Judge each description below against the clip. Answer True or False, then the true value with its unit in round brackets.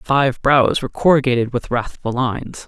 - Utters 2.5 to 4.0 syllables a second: False (4.9 syllables/s)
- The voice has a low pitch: True (130 Hz)